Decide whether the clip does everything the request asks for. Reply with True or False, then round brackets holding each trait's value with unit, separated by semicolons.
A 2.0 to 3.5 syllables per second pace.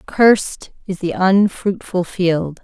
True (3.4 syllables/s)